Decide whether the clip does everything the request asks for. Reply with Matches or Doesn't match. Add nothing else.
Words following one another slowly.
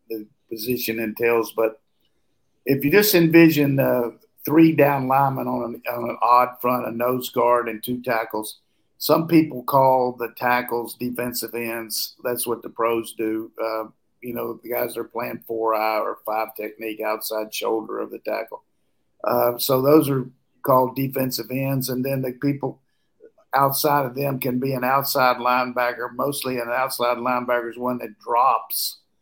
Doesn't match